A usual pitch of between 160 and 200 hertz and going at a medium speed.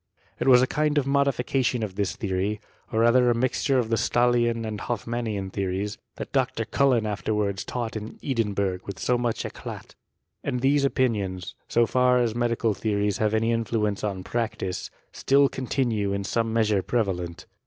No: low, 115 Hz; average, 160 wpm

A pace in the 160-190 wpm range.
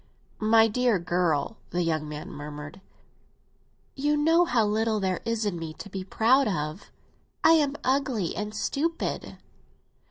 No: average, 145 wpm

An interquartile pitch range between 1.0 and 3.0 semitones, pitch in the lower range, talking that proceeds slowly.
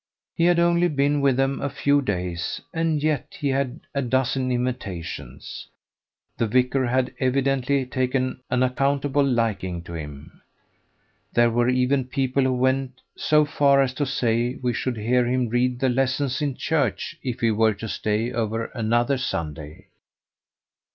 No: average, 2.7 semitones; low, 130 Hz; average, 155 wpm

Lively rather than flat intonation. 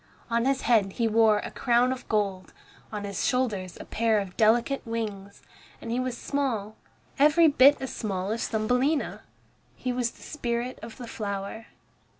No: average, 3.3 semitones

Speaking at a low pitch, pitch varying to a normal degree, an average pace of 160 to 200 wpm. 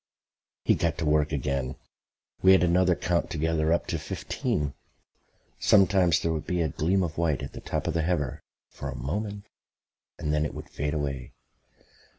Yes: very low, 80 Hz; average, 3.0 semitones; average, 175 wpm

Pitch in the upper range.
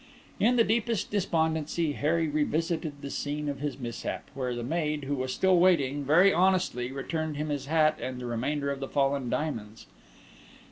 No: medium, 150 Hz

